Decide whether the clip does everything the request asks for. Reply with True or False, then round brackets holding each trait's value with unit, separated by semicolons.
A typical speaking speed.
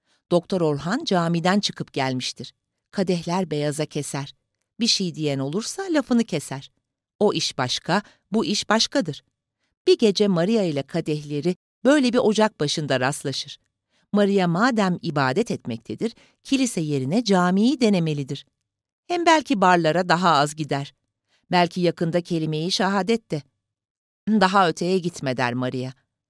True (125 wpm)